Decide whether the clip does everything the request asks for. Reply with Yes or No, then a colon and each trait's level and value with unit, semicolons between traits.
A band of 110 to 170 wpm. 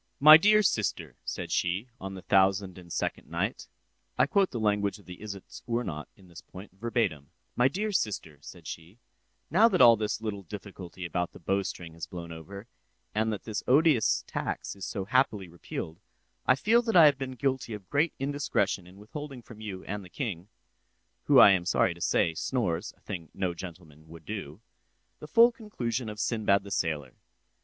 No: average, 180 wpm